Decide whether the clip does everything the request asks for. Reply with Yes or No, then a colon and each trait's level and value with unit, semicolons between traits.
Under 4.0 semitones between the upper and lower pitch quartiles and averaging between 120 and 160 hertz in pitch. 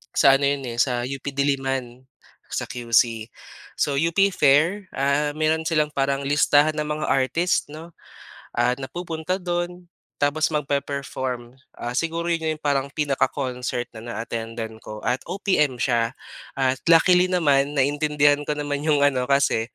Yes: average, 3.2 semitones; medium, 140 Hz